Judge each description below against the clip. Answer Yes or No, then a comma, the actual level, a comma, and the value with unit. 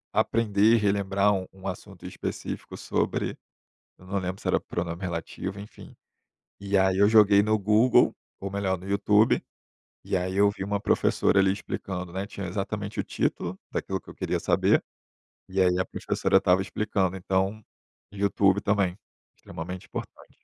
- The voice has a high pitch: No, very low, 95 Hz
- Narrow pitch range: Yes, narrow, 1.5 semitones